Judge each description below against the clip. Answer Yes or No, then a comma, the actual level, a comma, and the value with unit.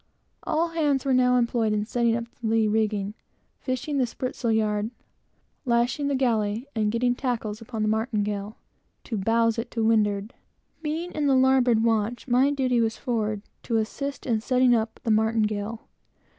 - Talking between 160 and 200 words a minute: Yes, average, 165 wpm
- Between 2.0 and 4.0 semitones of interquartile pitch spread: Yes, average, 2.8 semitones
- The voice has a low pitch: No, high, 230 Hz